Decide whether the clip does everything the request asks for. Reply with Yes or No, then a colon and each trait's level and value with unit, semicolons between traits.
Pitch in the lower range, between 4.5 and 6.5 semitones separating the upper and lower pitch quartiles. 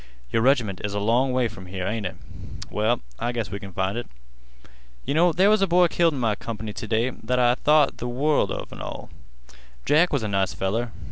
Yes: low, 120 Hz; average, 5.3 semitones